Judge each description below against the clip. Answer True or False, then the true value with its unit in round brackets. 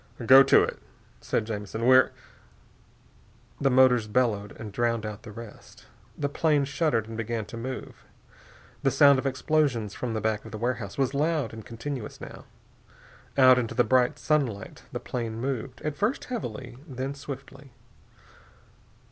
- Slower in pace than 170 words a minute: True (155 wpm)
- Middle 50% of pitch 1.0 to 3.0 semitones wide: False (3.5 semitones)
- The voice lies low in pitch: True (125 Hz)